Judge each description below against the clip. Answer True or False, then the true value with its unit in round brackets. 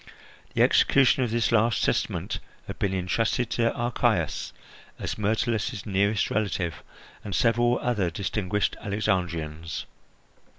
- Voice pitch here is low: True (105 Hz)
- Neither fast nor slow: False (115 wpm)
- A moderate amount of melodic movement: True (3.7 semitones)